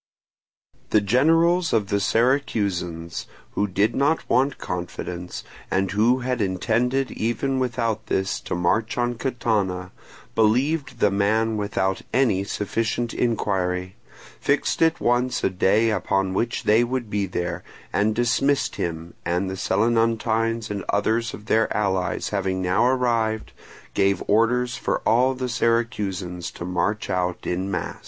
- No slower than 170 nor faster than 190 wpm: No, slow, 135 wpm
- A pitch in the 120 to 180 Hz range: No, low, 110 Hz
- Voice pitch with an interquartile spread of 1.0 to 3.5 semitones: No, average, 4.2 semitones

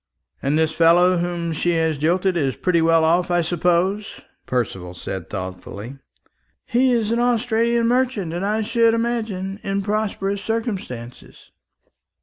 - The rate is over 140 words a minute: No, slow, 135 wpm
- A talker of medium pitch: Yes, medium, 180 Hz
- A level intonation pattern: No, wide, 5.5 semitones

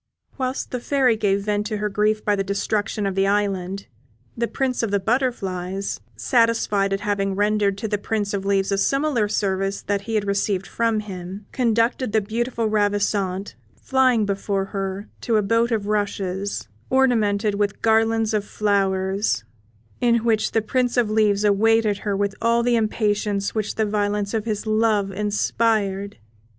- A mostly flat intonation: Yes, narrow, 2.2 semitones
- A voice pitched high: Yes, high, 210 Hz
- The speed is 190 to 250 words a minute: No, average, 165 wpm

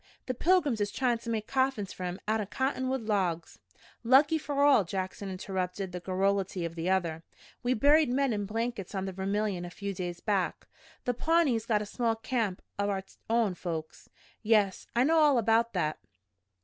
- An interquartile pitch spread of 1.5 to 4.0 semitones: No, average, 4.7 semitones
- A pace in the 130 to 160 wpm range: No, average, 180 wpm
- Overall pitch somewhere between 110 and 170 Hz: No, high, 210 Hz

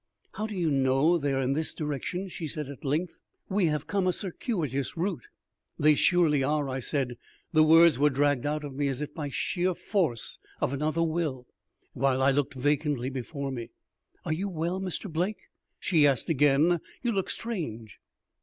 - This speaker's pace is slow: No, average, 180 wpm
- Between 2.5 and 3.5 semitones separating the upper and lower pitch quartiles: No, average, 4.1 semitones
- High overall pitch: No, medium, 150 Hz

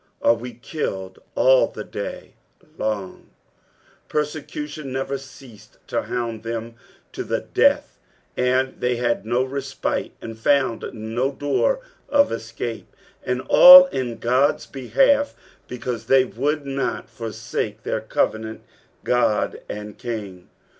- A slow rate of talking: Yes, slow, 120 wpm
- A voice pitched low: Yes, low, 125 Hz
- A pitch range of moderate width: Yes, average, 3.7 semitones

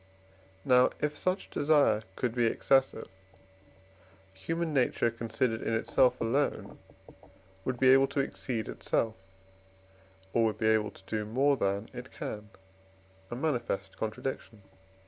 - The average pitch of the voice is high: No, low, 120 Hz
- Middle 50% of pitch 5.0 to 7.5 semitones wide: No, average, 3.5 semitones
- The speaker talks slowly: Yes, slow, 125 wpm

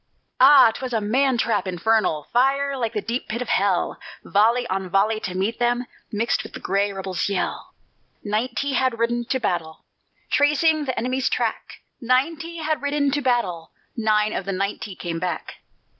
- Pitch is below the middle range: No, high, 230 Hz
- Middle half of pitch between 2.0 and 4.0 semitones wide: No, average, 4.8 semitones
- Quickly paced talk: No, average, 175 wpm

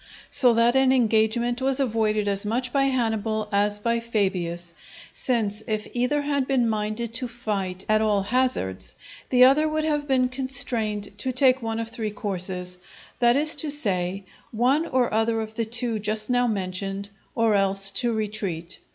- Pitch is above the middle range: Yes, high, 225 Hz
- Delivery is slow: No, average, 170 wpm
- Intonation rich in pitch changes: No, average, 3.6 semitones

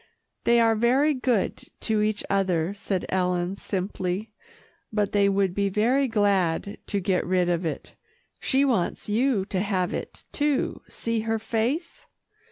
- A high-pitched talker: Yes, high, 205 Hz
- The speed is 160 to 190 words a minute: No, average, 150 wpm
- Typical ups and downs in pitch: Yes, average, 3.7 semitones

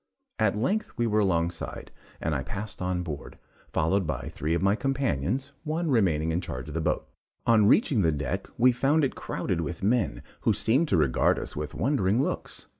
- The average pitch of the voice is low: Yes, very low, 95 Hz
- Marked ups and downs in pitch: Yes, wide, 7.5 semitones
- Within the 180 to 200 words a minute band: Yes, average, 190 wpm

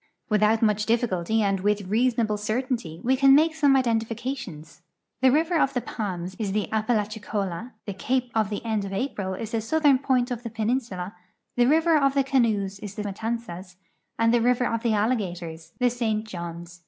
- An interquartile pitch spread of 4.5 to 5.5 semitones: No, average, 3.8 semitones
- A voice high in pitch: Yes, high, 220 Hz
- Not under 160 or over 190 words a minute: Yes, average, 185 wpm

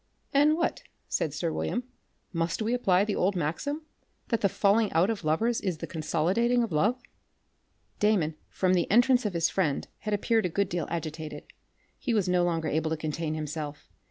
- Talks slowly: No, average, 185 wpm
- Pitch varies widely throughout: Yes, wide, 5.8 semitones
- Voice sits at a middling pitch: Yes, medium, 180 Hz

